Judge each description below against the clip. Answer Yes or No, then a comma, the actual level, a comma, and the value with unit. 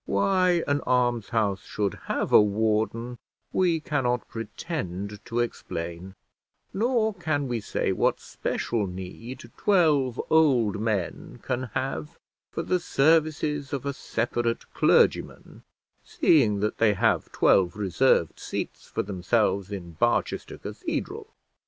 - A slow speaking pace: Yes, slow, 120 wpm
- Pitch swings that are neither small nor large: No, wide, 6.1 semitones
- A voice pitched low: Yes, low, 120 Hz